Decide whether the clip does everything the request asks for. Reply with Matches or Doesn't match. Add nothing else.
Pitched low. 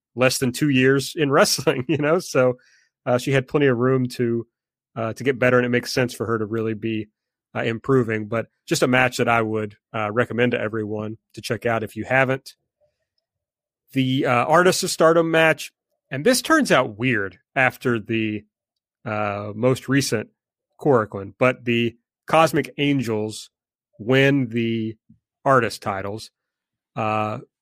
Matches